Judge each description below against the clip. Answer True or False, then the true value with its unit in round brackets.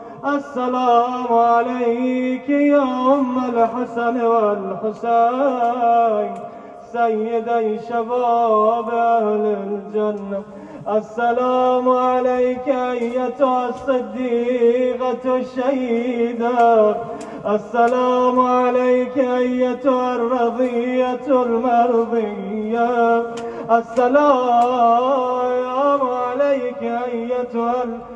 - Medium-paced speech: False (50 wpm)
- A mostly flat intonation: True (1.4 semitones)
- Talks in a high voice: True (240 Hz)